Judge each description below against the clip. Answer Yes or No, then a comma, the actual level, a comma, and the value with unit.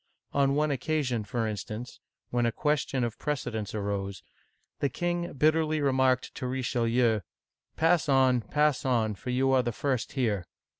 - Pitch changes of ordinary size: Yes, average, 3.8 semitones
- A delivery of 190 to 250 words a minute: No, average, 150 wpm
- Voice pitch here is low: Yes, low, 130 Hz